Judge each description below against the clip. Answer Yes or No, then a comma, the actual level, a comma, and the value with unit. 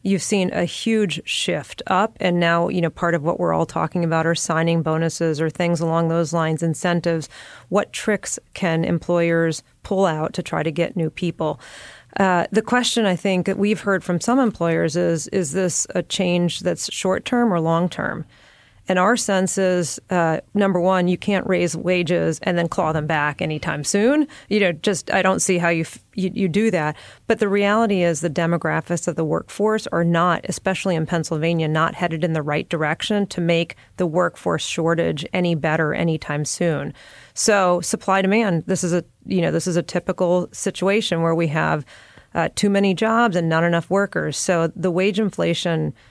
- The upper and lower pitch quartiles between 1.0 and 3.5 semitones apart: Yes, narrow, 2.6 semitones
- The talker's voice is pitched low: No, medium, 175 Hz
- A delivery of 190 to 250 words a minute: Yes, average, 195 wpm